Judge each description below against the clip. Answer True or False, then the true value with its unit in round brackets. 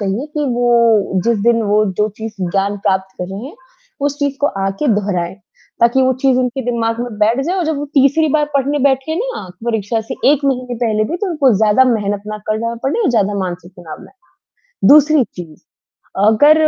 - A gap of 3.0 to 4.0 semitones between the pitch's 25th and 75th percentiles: False (5.2 semitones)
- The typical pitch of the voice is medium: False (235 Hz)